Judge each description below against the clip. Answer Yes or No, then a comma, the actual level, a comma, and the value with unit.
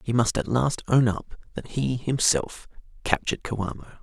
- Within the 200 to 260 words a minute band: No, average, 165 wpm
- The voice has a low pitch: Yes, low, 120 Hz